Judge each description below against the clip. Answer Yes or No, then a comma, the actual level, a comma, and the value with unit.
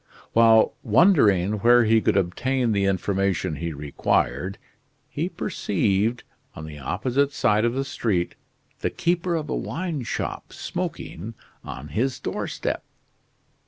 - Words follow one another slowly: Yes, slow, 125 wpm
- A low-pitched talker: Yes, low, 110 Hz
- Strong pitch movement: Yes, wide, 6.0 semitones